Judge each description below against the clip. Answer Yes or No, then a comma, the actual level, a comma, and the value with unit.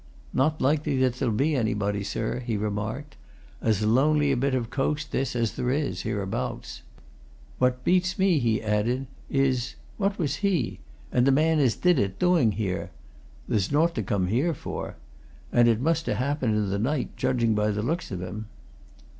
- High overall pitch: No, low, 125 Hz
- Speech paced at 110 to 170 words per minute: No, average, 180 wpm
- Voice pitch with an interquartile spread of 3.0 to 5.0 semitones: No, wide, 5.5 semitones